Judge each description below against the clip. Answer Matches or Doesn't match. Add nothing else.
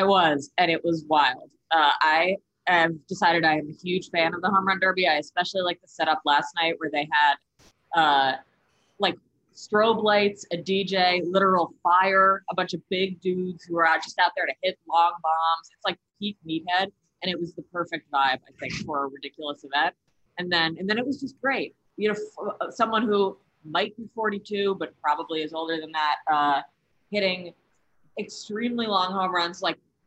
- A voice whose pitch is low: Doesn't match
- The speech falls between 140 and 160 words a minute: Doesn't match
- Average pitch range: Matches